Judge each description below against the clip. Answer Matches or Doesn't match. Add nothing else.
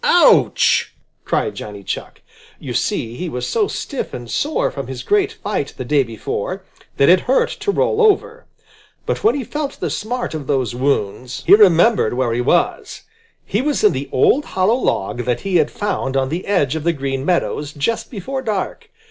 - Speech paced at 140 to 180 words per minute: Doesn't match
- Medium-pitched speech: Matches